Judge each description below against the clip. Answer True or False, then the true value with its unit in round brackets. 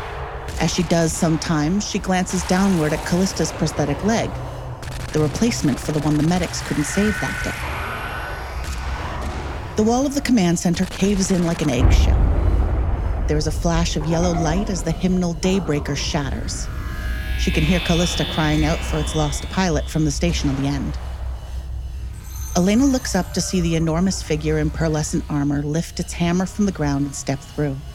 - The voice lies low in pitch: False (155 Hz)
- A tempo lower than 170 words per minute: False (175 wpm)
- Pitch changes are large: True (6.3 semitones)